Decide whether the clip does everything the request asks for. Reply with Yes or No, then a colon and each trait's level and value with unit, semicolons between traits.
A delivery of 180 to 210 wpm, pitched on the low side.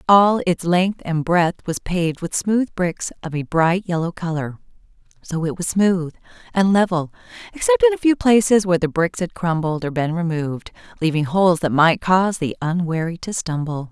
No: average, 185 wpm; medium, 175 Hz